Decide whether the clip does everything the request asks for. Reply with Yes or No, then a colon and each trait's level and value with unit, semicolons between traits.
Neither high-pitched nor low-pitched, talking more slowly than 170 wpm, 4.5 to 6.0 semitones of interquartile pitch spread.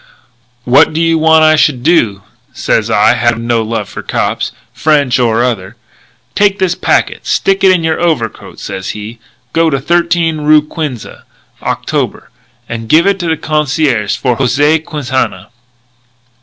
Yes: medium, 150 Hz; average, 160 wpm; wide, 5.5 semitones